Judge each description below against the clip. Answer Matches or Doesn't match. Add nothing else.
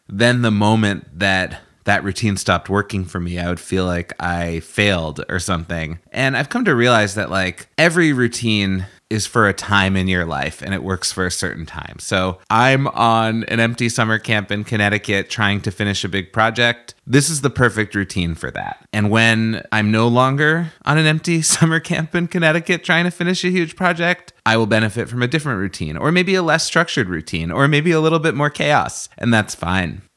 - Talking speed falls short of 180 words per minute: Doesn't match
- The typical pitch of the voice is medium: Doesn't match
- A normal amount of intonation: Doesn't match